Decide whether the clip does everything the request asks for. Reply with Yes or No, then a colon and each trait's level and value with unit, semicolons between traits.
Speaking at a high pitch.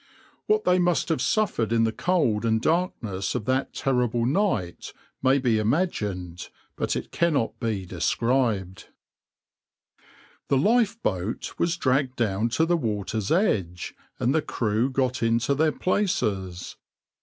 No: low, 125 Hz